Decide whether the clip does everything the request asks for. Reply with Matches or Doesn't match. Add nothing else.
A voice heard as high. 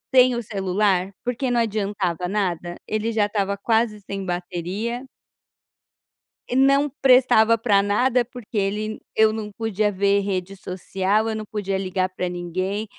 Matches